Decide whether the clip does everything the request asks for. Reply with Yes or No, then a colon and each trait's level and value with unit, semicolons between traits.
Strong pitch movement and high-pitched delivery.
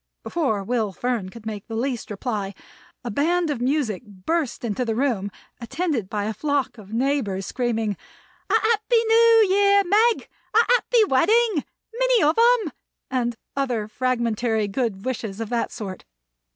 Yes: wide, 8.3 semitones; very high, 250 Hz